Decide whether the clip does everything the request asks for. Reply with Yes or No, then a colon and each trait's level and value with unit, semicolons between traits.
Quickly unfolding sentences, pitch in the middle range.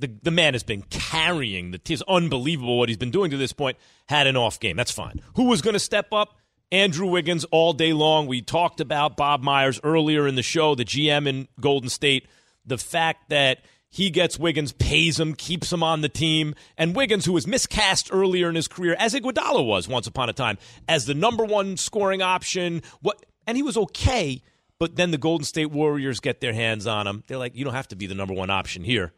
Yes: fast, 225 wpm; medium, 155 Hz